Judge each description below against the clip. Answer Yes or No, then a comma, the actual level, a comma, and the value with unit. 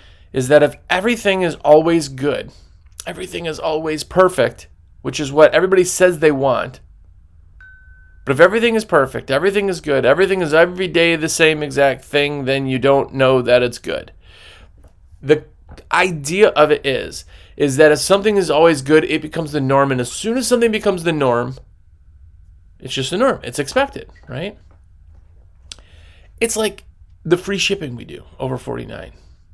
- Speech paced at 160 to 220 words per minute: Yes, average, 165 wpm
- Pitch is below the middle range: No, medium, 145 Hz